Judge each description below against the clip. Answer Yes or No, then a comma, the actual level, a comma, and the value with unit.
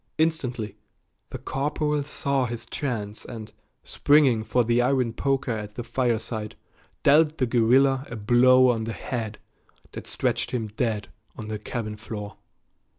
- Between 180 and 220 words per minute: No, average, 145 wpm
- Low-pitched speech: Yes, low, 120 Hz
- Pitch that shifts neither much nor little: Yes, average, 3.5 semitones